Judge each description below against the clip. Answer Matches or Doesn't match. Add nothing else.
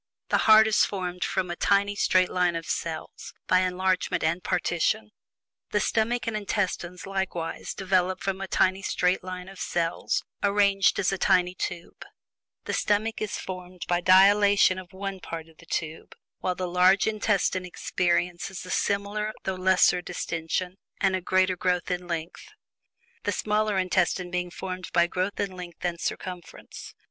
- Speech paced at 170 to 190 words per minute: Doesn't match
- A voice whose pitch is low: Doesn't match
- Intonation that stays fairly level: Matches